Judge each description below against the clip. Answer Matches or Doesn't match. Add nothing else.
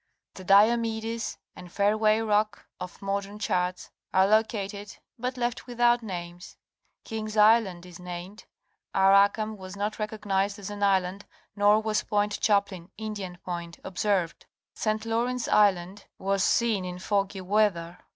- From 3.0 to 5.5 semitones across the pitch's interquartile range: Doesn't match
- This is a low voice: Doesn't match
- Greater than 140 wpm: Doesn't match